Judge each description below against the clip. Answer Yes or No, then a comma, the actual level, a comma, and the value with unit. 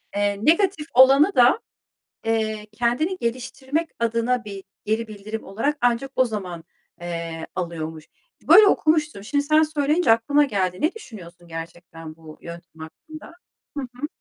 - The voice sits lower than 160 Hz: No, high, 230 Hz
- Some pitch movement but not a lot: No, wide, 8.1 semitones